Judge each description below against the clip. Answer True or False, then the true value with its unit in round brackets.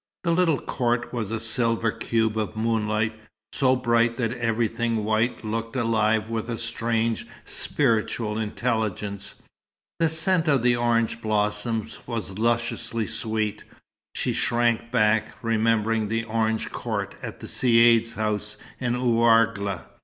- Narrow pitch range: True (1.4 semitones)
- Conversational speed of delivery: False (130 wpm)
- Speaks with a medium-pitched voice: False (115 Hz)